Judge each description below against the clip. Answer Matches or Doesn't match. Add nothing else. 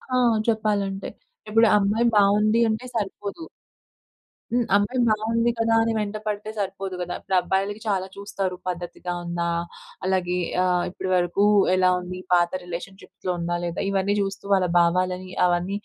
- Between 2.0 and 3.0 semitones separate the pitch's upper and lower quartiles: Matches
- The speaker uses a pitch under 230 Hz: Matches